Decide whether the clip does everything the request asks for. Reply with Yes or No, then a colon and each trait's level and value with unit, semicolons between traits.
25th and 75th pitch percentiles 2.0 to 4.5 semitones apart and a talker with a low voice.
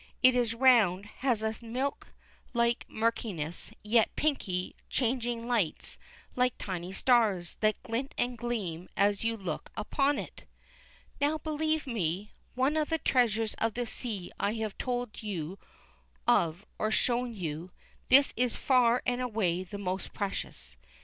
No: average, 4.0 semitones; high, 230 Hz